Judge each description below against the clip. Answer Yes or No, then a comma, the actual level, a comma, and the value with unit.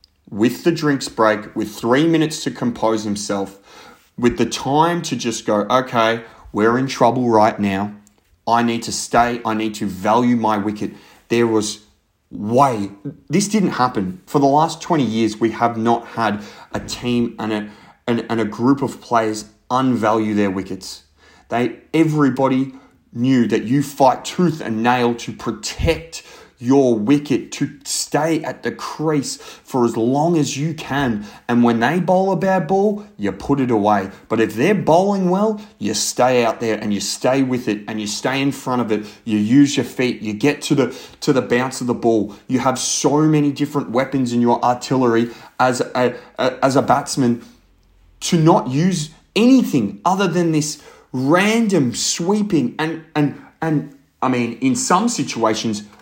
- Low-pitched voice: Yes, low, 125 Hz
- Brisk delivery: No, average, 175 wpm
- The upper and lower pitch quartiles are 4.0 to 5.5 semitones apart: Yes, average, 5.1 semitones